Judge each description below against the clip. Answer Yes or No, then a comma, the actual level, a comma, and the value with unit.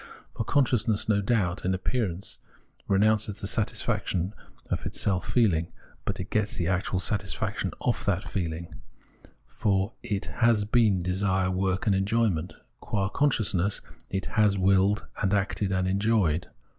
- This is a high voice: No, low, 100 Hz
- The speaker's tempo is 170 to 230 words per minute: No, average, 150 wpm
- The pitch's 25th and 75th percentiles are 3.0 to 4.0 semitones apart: No, narrow, 2.5 semitones